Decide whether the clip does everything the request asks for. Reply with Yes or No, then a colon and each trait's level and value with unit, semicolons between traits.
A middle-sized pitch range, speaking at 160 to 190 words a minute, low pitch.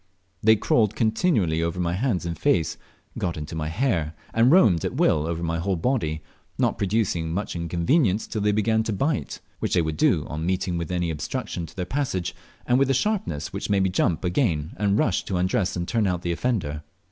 No: average, 4.9 semitones; fast, 205 wpm; very low, 90 Hz